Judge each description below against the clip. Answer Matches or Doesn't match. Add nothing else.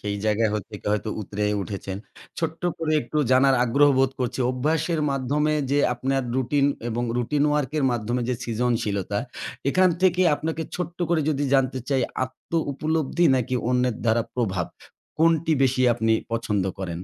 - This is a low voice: Matches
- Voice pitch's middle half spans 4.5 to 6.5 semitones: Matches